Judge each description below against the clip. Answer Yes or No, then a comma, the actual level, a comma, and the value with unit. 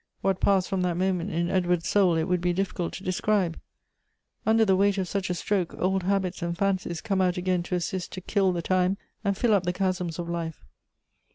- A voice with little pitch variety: Yes, narrow, 1.8 semitones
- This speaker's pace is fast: Yes, fast, 215 wpm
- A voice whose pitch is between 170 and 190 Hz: Yes, medium, 185 Hz